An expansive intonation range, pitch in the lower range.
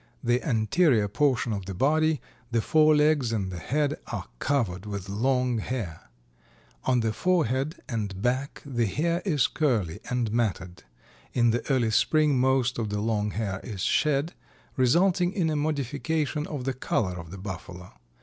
Yes: wide, 6.0 semitones; low, 125 Hz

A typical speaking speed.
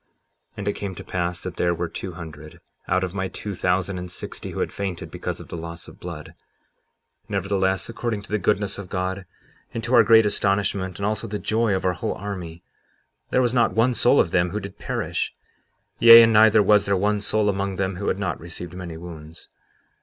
No: fast, 215 wpm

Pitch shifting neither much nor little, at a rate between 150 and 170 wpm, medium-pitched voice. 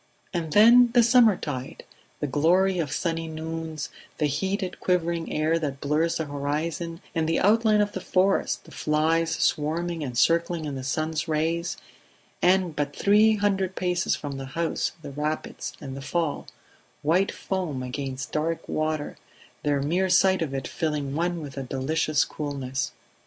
Yes: average, 3.5 semitones; average, 155 wpm; medium, 160 Hz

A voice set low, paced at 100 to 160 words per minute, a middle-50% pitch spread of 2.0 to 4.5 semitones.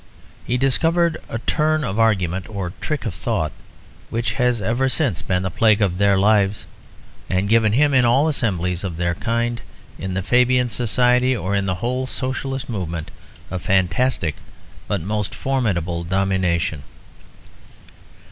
No: low, 110 Hz; average, 145 wpm; average, 5.1 semitones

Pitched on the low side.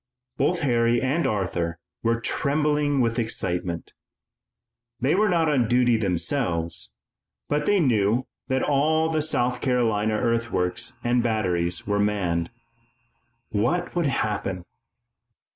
Yes: low, 120 Hz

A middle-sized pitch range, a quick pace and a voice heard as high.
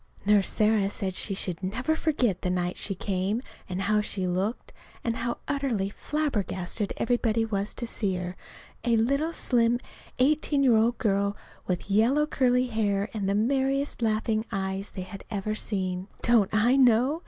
No: average, 3.9 semitones; average, 165 wpm; high, 215 Hz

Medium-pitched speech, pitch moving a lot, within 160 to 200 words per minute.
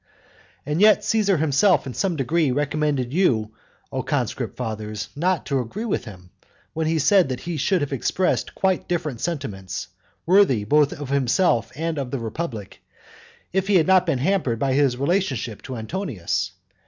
Yes: medium, 145 Hz; wide, 6.4 semitones; average, 165 wpm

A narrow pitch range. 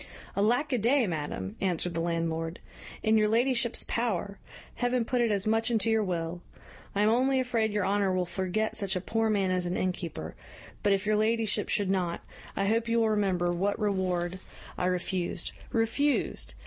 No: average, 3.8 semitones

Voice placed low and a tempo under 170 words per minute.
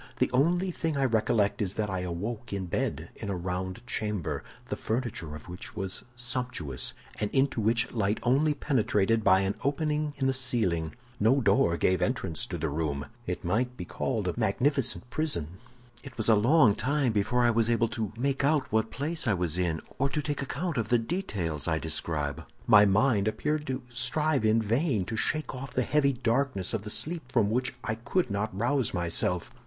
No: low, 115 Hz; average, 195 wpm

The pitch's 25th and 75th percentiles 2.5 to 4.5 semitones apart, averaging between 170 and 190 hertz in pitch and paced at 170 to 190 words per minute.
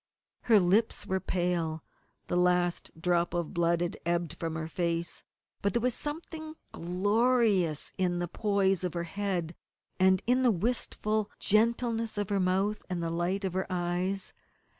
No: average, 3.6 semitones; medium, 185 Hz; average, 160 wpm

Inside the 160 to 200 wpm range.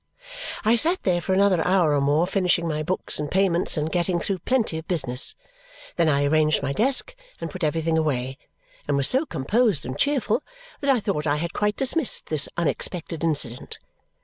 Yes: average, 185 wpm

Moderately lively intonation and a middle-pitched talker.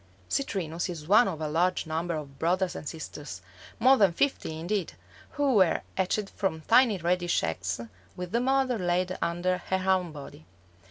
Yes: average, 3.8 semitones; medium, 180 Hz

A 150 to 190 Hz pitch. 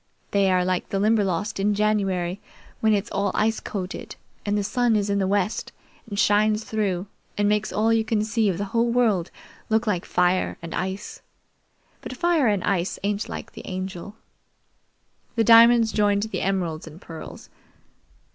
No: high, 205 Hz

